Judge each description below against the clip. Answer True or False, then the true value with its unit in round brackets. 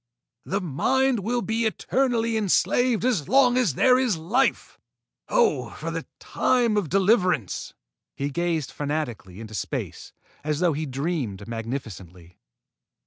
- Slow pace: True (130 wpm)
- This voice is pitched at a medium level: True (180 Hz)